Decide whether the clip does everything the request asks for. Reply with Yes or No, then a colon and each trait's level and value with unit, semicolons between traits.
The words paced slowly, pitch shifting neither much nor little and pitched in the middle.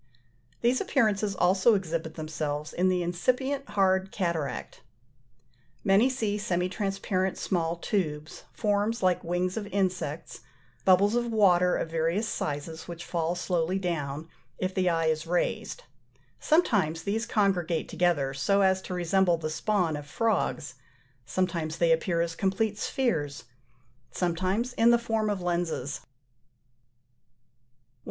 Yes: slow, 130 wpm; average, 3.7 semitones; medium, 180 Hz